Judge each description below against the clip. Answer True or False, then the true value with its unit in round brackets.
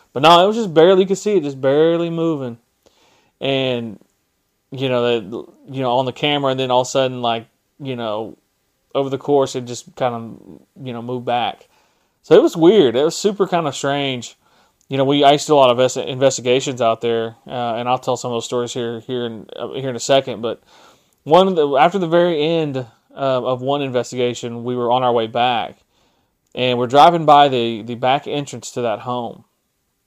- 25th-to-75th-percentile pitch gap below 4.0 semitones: True (2.9 semitones)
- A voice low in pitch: True (130 Hz)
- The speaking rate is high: True (220 wpm)